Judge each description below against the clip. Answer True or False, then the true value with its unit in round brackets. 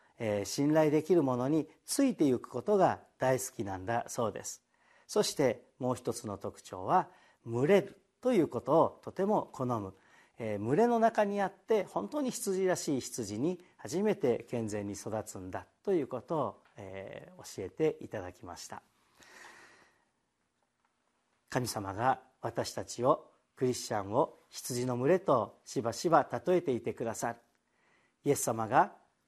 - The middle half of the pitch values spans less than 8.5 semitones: False (9.0 semitones)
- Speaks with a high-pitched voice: False (130 Hz)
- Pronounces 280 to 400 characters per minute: False (265 characters per minute)